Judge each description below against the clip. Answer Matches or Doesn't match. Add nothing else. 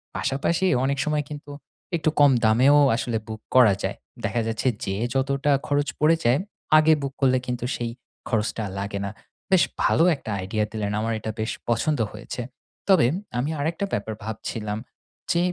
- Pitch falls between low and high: Doesn't match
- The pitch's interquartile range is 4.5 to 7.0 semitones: Matches